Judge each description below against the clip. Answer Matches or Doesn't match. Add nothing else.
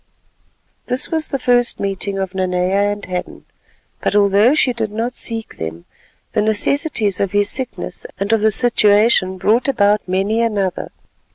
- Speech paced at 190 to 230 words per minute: Doesn't match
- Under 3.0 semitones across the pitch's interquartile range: Doesn't match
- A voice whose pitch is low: Doesn't match